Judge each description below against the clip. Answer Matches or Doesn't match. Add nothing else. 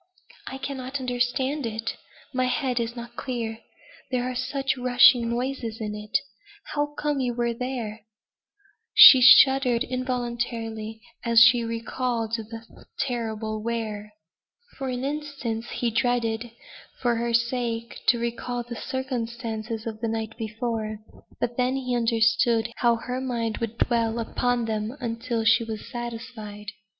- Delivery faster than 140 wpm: Doesn't match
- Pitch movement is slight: Matches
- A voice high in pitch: Matches